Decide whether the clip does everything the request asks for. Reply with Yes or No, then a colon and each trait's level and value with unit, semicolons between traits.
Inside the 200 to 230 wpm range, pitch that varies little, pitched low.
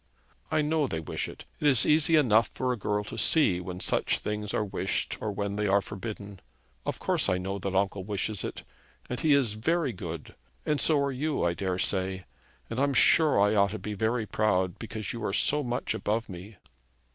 No: fast, 205 wpm; average, 4.7 semitones; low, 105 Hz